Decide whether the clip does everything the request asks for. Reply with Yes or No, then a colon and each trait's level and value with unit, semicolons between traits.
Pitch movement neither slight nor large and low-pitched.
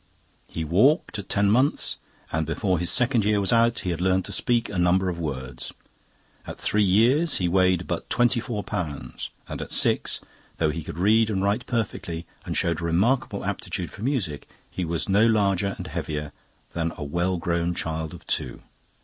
Yes: average, 4.6 semitones; very low, 95 Hz